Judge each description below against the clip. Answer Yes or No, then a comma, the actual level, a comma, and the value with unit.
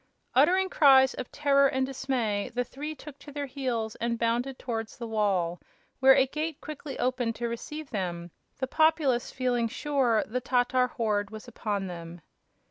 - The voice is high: Yes, very high, 250 Hz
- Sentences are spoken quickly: No, average, 165 wpm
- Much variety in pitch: No, average, 3.7 semitones